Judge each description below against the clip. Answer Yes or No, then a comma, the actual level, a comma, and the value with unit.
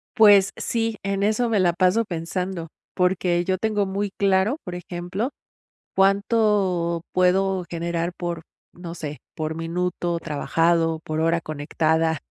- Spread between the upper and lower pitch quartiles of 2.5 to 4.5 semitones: Yes, average, 2.8 semitones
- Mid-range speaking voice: Yes, medium, 180 Hz